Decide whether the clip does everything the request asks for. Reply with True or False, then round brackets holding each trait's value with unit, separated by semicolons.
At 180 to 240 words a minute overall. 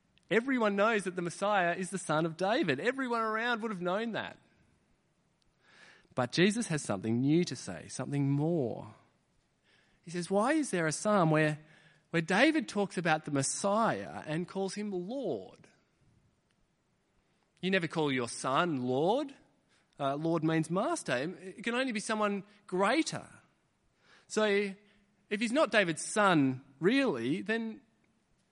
False (140 wpm)